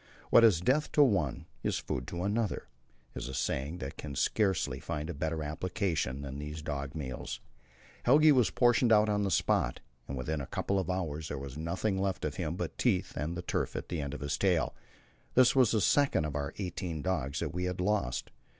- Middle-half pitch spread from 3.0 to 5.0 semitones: No, wide, 5.6 semitones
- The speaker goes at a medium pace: No, fast, 215 wpm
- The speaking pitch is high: No, very low, 85 Hz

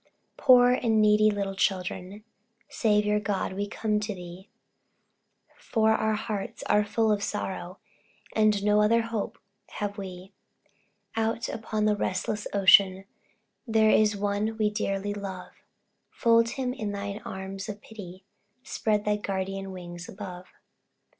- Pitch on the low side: No, high, 210 Hz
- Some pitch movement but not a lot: No, narrow, 1.9 semitones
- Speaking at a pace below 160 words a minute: Yes, slow, 135 wpm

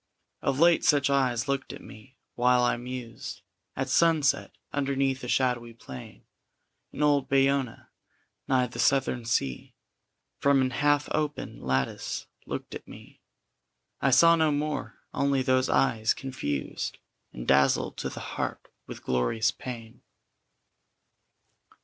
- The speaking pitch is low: Yes, low, 130 Hz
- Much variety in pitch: No, average, 3.1 semitones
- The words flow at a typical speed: No, slow, 130 wpm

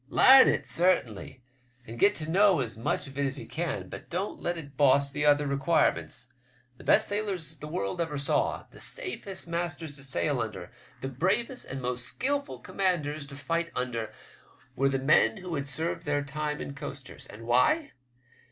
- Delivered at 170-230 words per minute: Yes, average, 180 wpm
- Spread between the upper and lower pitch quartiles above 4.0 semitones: Yes, average, 4.4 semitones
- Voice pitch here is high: No, medium, 145 Hz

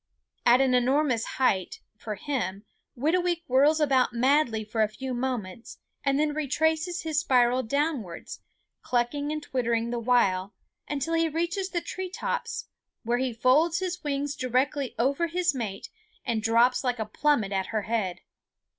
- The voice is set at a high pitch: Yes, very high, 260 Hz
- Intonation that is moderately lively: Yes, average, 4.8 semitones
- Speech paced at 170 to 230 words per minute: No, average, 155 wpm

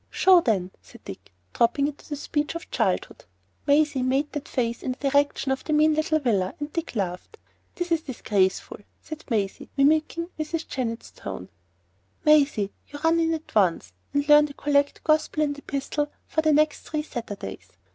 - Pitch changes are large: No, average, 4.3 semitones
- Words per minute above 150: Yes, average, 175 wpm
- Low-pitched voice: No, very high, 290 Hz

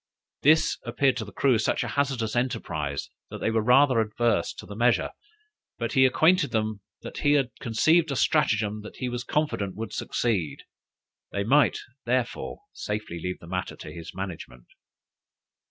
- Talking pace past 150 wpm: Yes, average, 165 wpm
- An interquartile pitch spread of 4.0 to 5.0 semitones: Yes, average, 4.5 semitones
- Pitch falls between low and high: No, low, 115 Hz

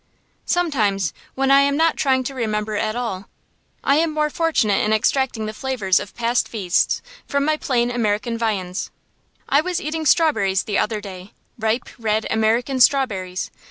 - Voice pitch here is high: Yes, high, 230 Hz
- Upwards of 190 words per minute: No, average, 160 wpm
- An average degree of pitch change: Yes, average, 4.8 semitones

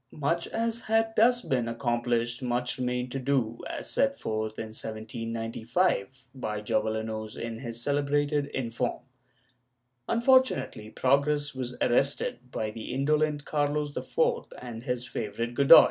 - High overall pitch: No, low, 125 Hz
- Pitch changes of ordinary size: Yes, average, 4.1 semitones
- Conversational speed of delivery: No, slow, 130 wpm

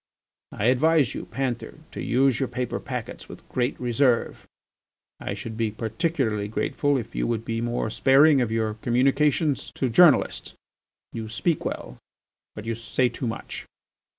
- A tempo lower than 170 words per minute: Yes, average, 150 wpm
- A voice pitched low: Yes, low, 120 Hz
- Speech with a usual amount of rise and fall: Yes, average, 3.3 semitones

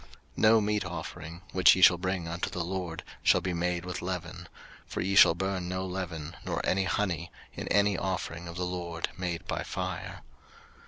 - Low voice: Yes, very low, 90 Hz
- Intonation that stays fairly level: Yes, narrow, 1.6 semitones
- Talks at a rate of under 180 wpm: No, average, 190 wpm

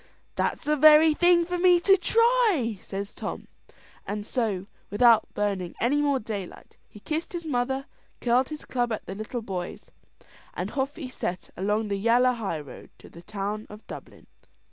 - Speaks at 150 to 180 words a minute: Yes, average, 165 wpm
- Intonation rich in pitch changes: Yes, wide, 6.7 semitones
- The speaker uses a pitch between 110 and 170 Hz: No, high, 240 Hz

